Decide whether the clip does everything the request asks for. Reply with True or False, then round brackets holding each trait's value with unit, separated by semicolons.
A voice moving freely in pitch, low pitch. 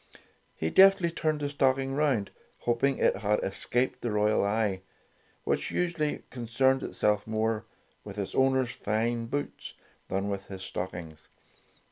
False (4.7 semitones; 115 Hz)